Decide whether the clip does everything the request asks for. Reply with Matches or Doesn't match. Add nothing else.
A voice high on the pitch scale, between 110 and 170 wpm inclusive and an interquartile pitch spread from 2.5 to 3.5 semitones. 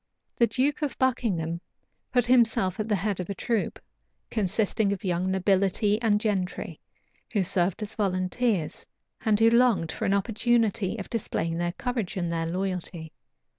Doesn't match